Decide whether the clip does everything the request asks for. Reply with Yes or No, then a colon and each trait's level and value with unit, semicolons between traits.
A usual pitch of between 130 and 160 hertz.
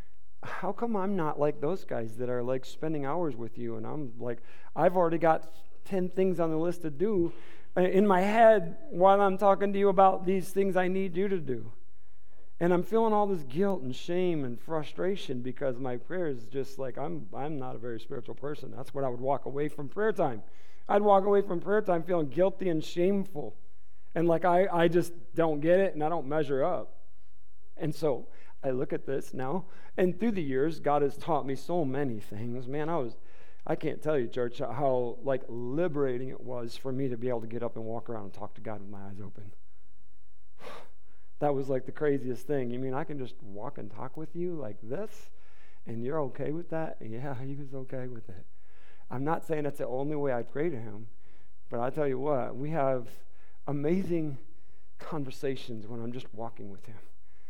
Yes: medium, 140 Hz